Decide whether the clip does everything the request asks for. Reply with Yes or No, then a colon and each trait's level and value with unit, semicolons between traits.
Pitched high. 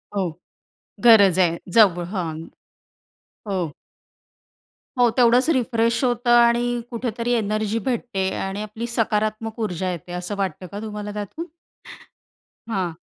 Yes: high, 215 Hz